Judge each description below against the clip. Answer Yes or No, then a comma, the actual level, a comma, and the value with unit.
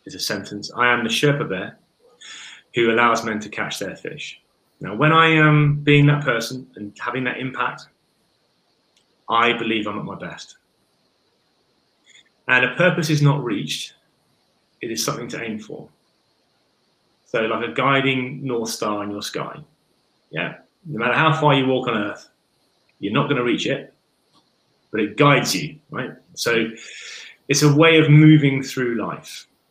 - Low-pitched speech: Yes, low, 130 Hz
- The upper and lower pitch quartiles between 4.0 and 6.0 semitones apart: Yes, average, 4.4 semitones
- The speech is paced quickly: No, average, 165 wpm